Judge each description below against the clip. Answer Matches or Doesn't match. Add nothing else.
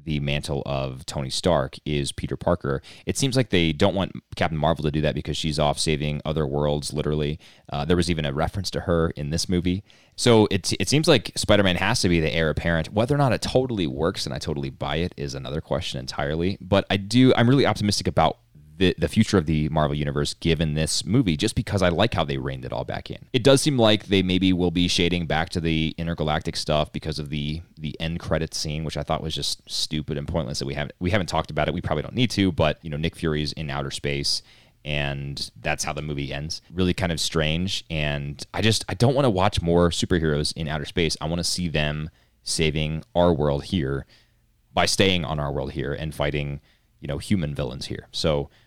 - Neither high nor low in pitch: Doesn't match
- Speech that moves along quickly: Matches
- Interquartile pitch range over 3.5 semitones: Matches